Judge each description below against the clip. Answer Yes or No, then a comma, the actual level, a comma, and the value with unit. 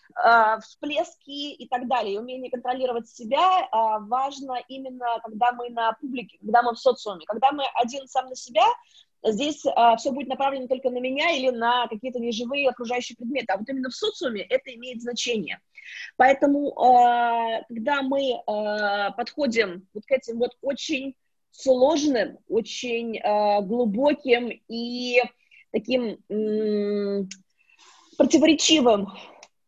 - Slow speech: No, average, 120 wpm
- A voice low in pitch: No, very high, 250 Hz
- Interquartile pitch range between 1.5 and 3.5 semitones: Yes, average, 3.1 semitones